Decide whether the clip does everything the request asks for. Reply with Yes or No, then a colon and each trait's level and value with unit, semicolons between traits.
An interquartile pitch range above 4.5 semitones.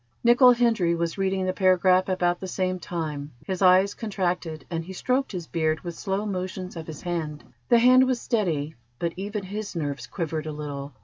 No: average, 3.5 semitones